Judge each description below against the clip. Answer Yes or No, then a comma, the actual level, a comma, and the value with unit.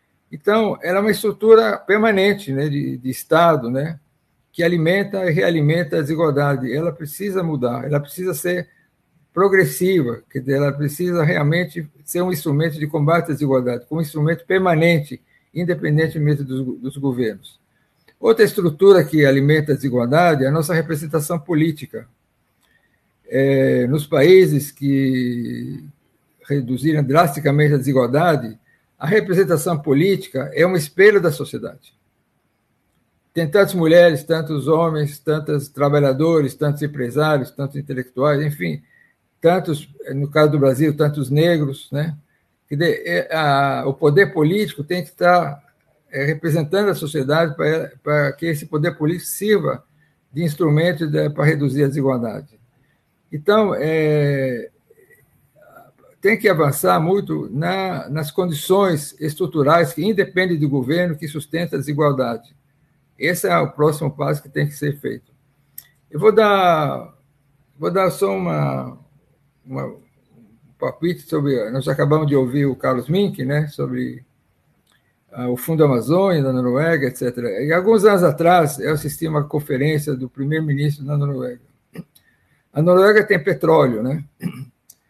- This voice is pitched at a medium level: Yes, medium, 150 Hz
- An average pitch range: Yes, average, 3.5 semitones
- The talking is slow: No, average, 130 wpm